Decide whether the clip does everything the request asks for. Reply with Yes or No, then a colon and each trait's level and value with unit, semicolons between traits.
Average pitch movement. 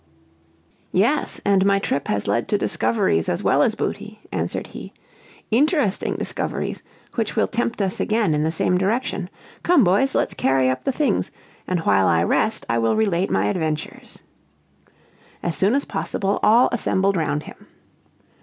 No: wide, 6.6 semitones